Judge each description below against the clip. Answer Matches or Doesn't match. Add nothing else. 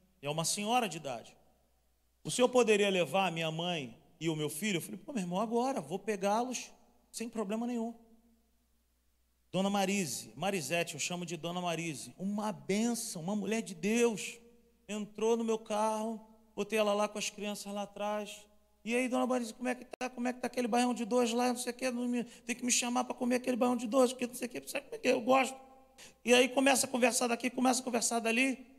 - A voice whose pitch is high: Matches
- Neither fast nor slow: Doesn't match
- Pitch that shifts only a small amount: Doesn't match